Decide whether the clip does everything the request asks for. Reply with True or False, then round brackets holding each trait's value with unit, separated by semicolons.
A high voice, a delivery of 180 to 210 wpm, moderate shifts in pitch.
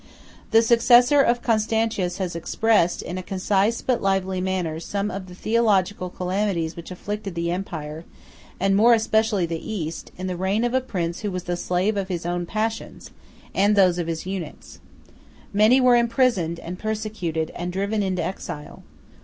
False (195 Hz; 170 wpm; 3.7 semitones)